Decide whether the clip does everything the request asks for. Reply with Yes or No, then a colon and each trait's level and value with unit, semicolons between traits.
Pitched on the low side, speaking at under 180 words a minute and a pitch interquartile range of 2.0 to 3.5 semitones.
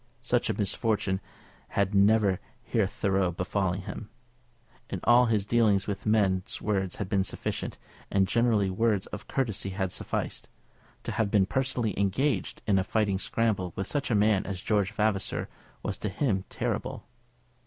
Yes: low, 100 Hz; average, 155 wpm; narrow, 2.5 semitones